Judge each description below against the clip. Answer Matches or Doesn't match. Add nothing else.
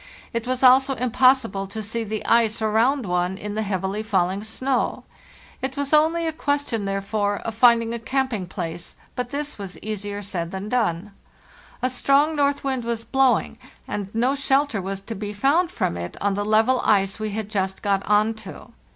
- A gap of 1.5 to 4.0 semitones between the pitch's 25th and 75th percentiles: Doesn't match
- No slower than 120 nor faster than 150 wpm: Doesn't match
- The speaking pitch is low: Doesn't match